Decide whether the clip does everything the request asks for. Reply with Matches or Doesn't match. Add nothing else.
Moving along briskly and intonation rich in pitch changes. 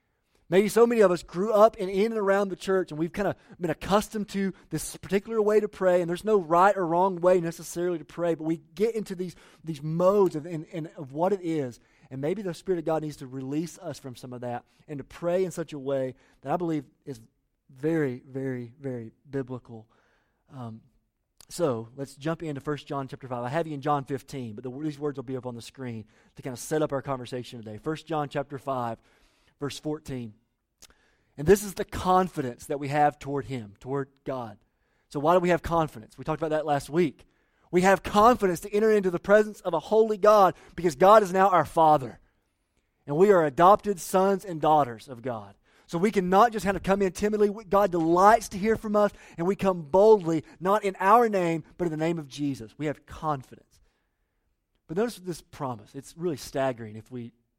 Matches